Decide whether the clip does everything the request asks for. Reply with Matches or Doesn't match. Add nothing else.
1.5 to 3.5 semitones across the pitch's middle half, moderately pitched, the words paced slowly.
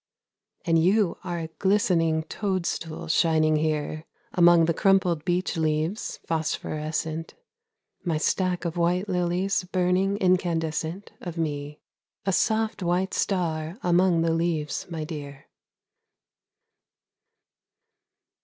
Matches